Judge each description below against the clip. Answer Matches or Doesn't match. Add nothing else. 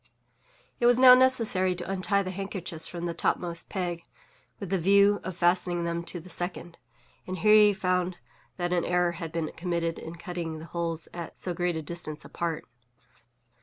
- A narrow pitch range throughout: Matches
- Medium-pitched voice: Matches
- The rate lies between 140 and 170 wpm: Doesn't match